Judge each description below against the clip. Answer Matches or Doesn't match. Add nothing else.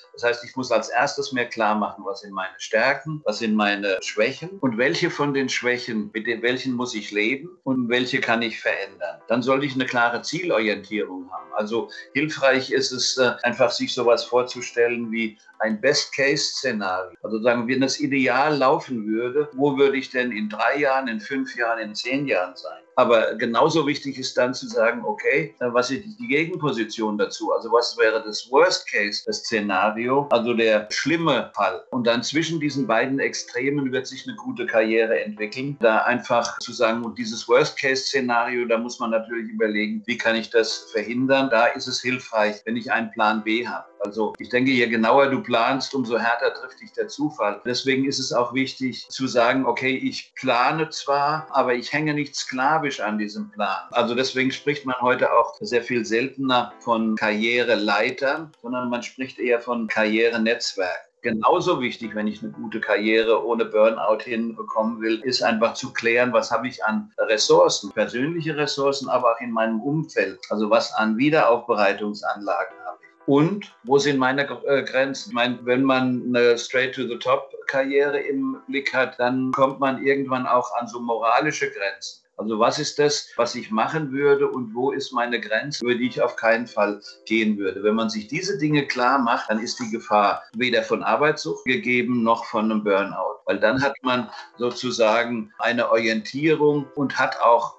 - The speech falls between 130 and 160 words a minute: Doesn't match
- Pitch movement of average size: Matches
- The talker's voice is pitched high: Doesn't match